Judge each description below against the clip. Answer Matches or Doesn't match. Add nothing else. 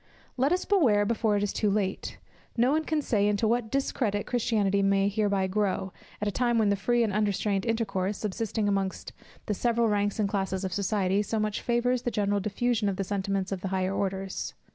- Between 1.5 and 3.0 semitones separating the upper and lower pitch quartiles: Matches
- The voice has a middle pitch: Doesn't match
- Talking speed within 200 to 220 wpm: Matches